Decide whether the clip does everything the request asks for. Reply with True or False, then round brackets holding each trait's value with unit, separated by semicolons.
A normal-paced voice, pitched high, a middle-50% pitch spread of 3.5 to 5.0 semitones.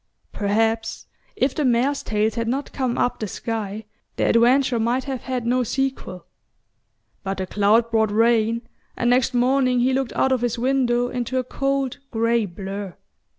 False (165 wpm; 240 Hz; 2.6 semitones)